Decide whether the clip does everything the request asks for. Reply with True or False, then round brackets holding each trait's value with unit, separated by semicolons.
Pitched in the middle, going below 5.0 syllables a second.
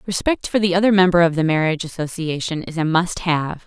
False (170 Hz; 6.0 syllables/s)